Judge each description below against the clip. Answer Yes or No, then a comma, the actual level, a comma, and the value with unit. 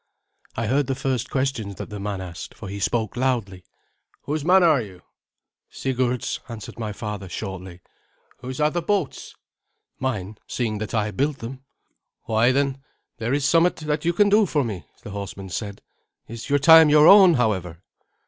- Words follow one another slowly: No, average, 170 wpm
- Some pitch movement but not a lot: No, wide, 6.0 semitones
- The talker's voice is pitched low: Yes, low, 120 Hz